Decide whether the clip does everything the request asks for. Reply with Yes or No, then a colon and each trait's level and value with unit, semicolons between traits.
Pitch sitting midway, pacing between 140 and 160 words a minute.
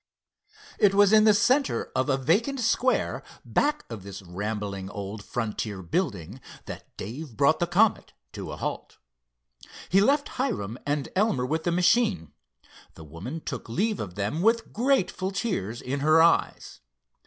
Yes: medium, 155 Hz; average, 155 wpm